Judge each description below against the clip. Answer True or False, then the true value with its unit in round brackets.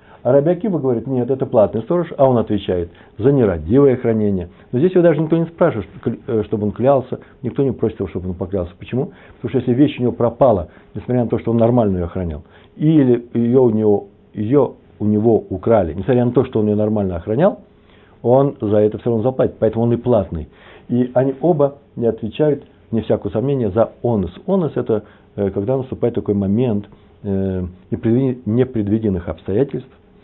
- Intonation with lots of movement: False (4.1 semitones)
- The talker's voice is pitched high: False (115 Hz)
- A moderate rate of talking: False (180 wpm)